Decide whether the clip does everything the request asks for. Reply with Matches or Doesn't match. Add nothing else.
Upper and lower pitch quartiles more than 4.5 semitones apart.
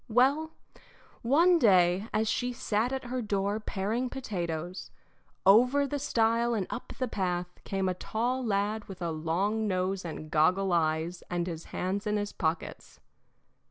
Matches